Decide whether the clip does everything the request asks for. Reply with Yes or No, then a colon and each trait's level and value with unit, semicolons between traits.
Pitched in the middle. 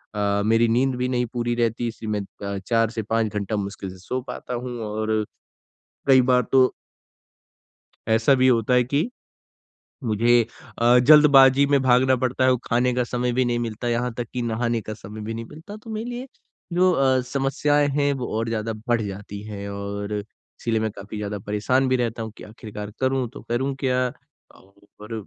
No: low, 120 Hz